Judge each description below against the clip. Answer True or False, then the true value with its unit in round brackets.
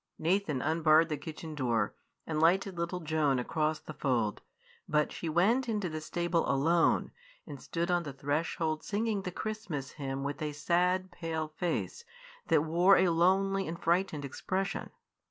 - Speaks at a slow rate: False (155 wpm)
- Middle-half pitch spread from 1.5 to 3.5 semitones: True (3.2 semitones)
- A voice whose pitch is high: False (165 Hz)